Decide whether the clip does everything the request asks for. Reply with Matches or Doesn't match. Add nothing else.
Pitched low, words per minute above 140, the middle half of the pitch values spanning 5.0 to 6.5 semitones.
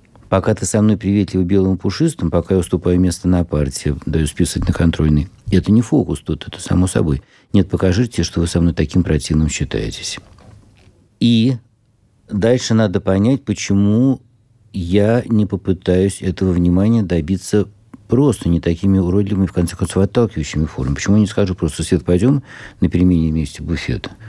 Doesn't match